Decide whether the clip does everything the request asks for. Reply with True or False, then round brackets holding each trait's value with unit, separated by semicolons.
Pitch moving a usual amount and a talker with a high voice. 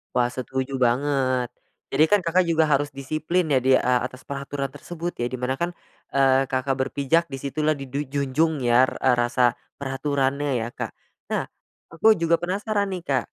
False (3.6 semitones; 140 Hz)